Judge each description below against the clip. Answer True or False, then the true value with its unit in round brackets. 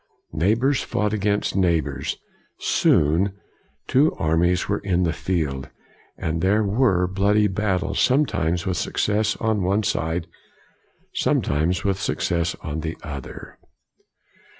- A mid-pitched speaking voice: False (90 Hz)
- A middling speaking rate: False (120 wpm)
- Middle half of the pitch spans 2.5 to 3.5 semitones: False (4.2 semitones)